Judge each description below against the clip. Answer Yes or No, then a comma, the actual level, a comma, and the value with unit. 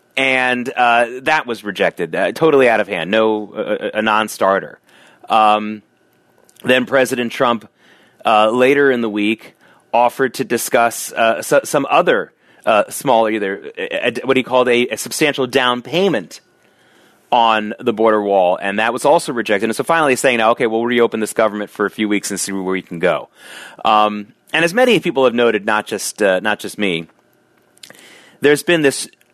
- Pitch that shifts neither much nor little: Yes, average, 3.3 semitones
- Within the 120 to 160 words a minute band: No, average, 180 wpm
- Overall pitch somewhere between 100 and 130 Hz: Yes, low, 115 Hz